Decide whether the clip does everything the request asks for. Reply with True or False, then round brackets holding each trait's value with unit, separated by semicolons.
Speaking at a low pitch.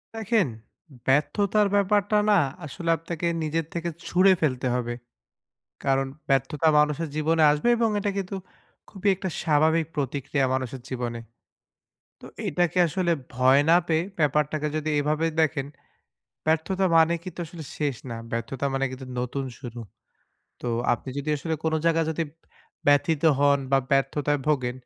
False (150 Hz)